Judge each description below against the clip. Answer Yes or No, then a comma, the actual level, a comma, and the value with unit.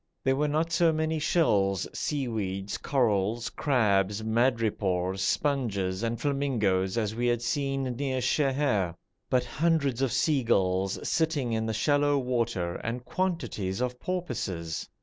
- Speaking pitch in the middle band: No, low, 120 Hz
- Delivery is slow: Yes, slow, 130 wpm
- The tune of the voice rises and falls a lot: Yes, wide, 6.1 semitones